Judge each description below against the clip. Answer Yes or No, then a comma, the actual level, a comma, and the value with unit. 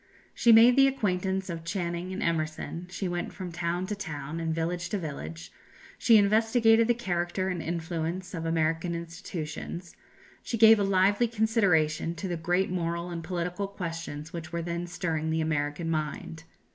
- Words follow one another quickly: No, average, 165 wpm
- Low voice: No, medium, 175 Hz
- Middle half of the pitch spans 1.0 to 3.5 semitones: Yes, average, 2.9 semitones